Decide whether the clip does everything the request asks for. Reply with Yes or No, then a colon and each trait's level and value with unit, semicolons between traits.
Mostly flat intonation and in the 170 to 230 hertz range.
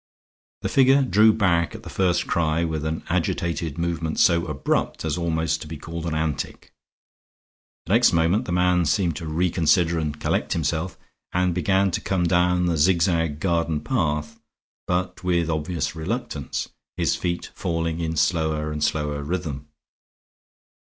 No: narrow, 2.3 semitones; very low, 85 Hz